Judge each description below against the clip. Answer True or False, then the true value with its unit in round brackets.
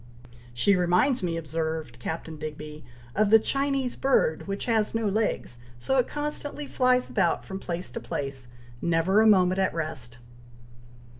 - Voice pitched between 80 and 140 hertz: False (185 Hz)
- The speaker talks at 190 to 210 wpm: False (150 wpm)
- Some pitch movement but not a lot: False (6.3 semitones)